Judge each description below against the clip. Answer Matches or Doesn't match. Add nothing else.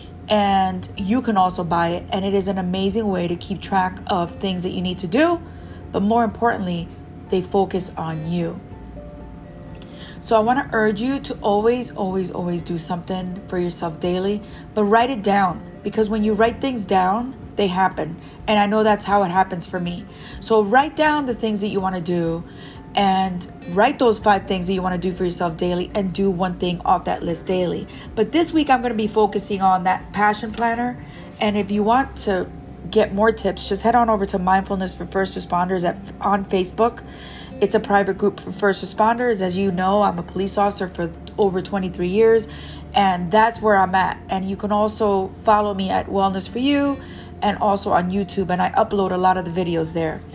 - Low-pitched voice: Doesn't match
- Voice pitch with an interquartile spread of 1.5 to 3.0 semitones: Matches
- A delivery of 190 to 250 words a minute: Matches